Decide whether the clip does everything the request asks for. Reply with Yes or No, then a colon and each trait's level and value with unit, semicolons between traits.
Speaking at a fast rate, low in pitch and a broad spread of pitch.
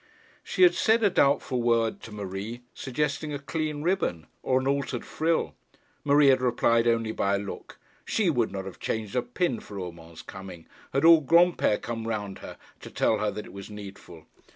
No: average, 190 wpm; low, 120 Hz; wide, 6.2 semitones